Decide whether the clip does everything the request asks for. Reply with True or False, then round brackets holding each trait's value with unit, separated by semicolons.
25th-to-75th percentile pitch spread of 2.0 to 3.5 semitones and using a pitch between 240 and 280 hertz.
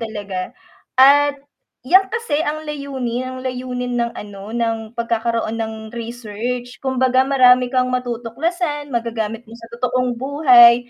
True (2.5 semitones; 245 Hz)